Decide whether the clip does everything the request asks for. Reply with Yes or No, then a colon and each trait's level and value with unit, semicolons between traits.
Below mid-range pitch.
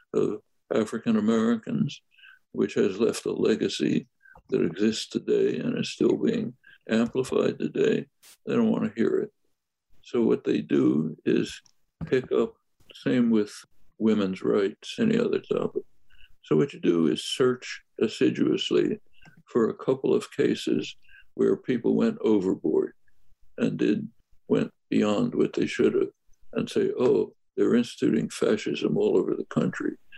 No: very high, 370 Hz